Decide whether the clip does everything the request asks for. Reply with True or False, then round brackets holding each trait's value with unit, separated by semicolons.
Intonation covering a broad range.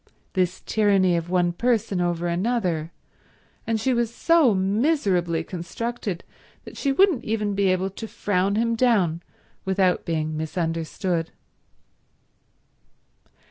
False (4.6 semitones)